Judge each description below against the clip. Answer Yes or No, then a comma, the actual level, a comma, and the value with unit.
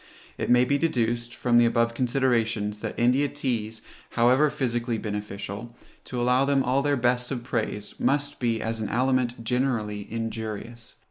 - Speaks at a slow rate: No, average, 155 wpm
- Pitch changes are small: Yes, narrow, 2.3 semitones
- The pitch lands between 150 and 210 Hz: No, low, 120 Hz